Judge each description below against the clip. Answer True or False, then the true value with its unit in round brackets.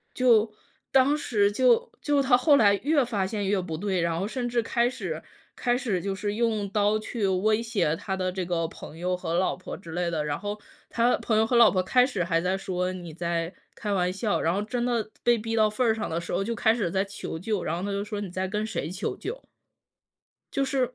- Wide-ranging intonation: False (4.3 semitones)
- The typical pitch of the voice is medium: False (205 Hz)